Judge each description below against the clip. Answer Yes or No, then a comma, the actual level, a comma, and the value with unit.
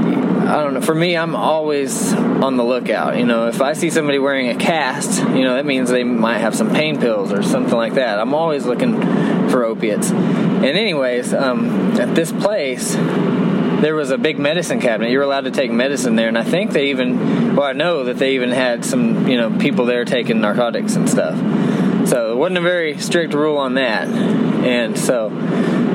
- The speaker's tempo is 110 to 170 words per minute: No, fast, 205 wpm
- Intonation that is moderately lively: No, wide, 8.3 semitones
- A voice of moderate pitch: Yes, medium, 165 Hz